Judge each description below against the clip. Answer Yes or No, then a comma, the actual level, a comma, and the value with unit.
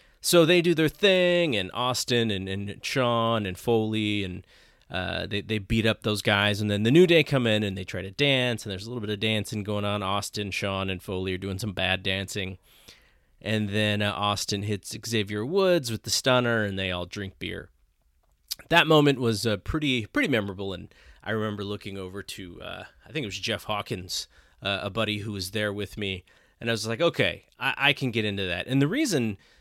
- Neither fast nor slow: No, fast, 215 wpm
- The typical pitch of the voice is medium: No, low, 105 Hz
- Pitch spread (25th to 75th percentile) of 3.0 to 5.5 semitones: Yes, average, 3.3 semitones